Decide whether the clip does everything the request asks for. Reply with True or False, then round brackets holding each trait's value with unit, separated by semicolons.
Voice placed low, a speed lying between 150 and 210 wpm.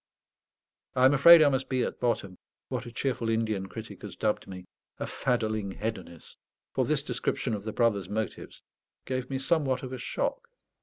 True (115 Hz; 175 wpm)